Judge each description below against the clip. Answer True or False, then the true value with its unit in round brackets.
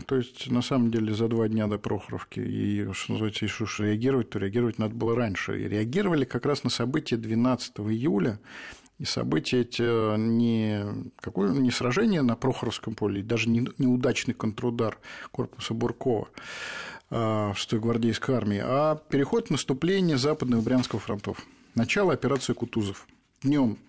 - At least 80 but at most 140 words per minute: False (150 wpm)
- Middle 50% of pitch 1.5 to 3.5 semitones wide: True (2.8 semitones)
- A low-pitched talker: True (115 Hz)